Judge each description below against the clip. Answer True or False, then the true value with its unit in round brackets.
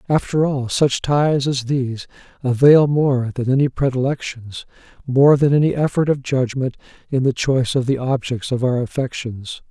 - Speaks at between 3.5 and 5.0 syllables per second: True (4.9 syllables/s)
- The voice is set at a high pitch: False (130 Hz)